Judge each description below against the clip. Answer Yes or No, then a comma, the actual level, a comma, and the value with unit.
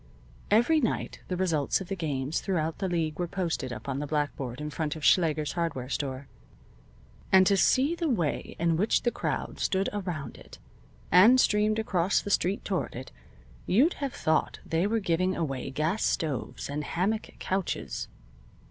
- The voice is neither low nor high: Yes, medium, 170 Hz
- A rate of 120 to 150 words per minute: No, average, 170 wpm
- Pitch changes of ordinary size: Yes, average, 4.9 semitones